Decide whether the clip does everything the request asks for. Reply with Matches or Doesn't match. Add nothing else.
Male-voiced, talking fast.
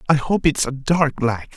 Matches